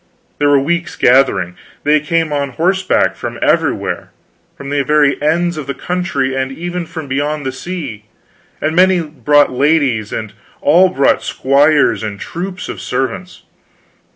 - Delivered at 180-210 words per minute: No, average, 150 wpm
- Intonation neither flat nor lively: Yes, average, 4.0 semitones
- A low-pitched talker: No, medium, 145 Hz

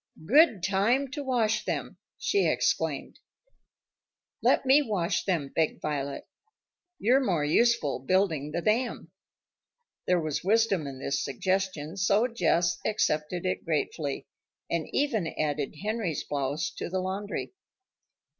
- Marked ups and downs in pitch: Yes, wide, 6.3 semitones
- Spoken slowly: Yes, slow, 125 wpm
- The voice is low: No, medium, 185 Hz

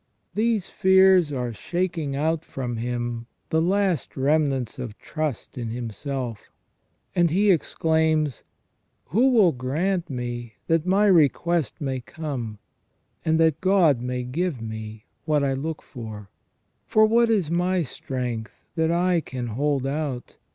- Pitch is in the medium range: Yes, medium, 150 Hz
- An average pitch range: No, wide, 5.9 semitones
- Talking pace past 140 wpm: No, slow, 135 wpm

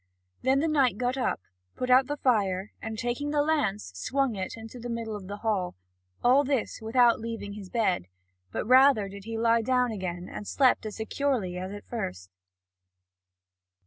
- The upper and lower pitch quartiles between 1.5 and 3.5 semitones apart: No, average, 4.1 semitones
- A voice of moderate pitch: No, high, 230 Hz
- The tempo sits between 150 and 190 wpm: Yes, average, 175 wpm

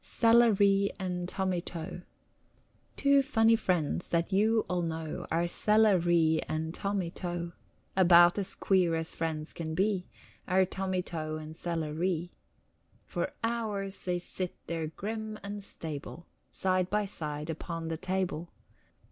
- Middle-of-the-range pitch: Yes, medium, 180 Hz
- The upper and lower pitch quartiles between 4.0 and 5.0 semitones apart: No, average, 3.3 semitones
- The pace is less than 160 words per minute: Yes, average, 140 wpm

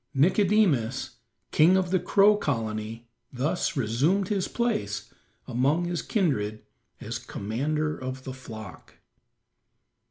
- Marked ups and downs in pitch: Yes, wide, 8.1 semitones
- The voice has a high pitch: No, medium, 140 Hz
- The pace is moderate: No, slow, 105 wpm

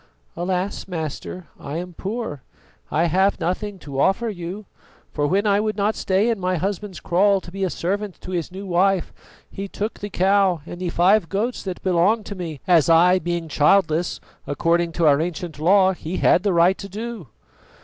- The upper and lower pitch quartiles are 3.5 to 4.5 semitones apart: No, average, 2.8 semitones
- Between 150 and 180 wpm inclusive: No, average, 190 wpm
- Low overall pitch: No, medium, 185 Hz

